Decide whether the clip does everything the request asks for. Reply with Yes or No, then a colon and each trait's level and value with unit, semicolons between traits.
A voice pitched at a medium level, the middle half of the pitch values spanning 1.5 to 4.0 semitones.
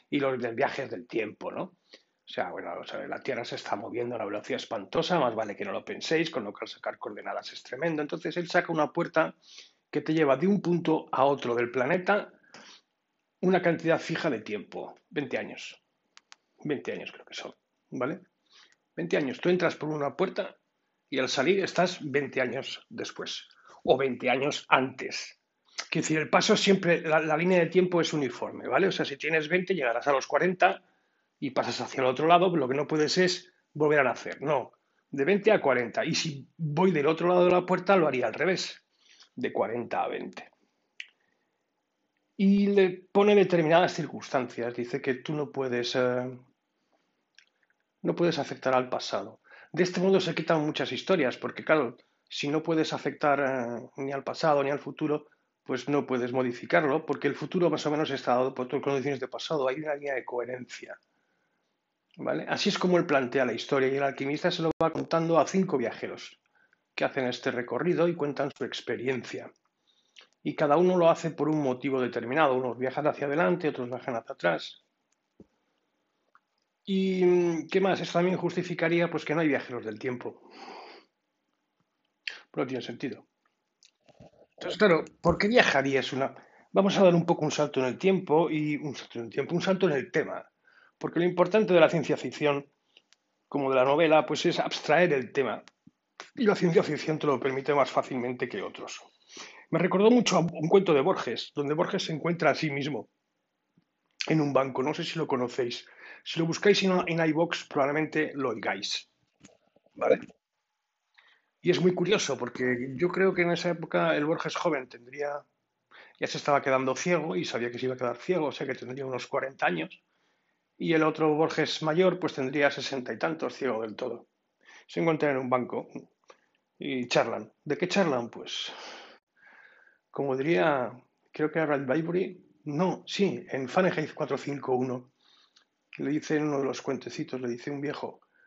No: medium, 155 Hz; average, 4.4 semitones